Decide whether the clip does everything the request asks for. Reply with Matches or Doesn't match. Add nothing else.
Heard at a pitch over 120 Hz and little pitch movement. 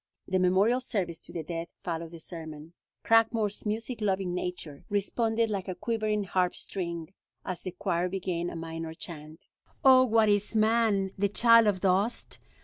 Doesn't match